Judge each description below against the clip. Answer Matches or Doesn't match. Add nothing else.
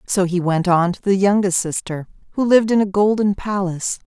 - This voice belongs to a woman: Matches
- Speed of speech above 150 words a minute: Matches